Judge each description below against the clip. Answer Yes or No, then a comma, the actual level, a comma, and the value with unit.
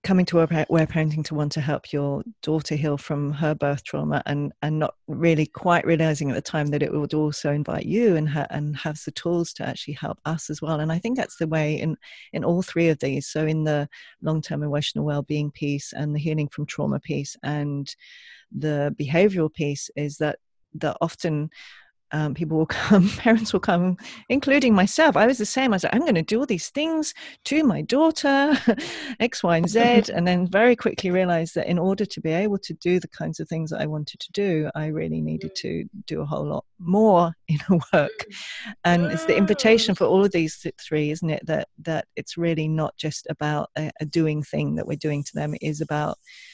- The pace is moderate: No, fast, 220 wpm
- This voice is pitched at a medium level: Yes, medium, 160 Hz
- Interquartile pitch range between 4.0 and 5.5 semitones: Yes, average, 4.3 semitones